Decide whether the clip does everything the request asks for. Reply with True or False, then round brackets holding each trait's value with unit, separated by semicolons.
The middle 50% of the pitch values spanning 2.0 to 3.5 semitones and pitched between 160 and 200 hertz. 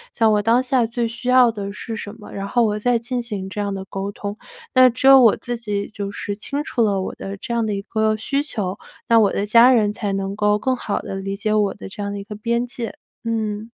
False (2.7 semitones; 215 Hz)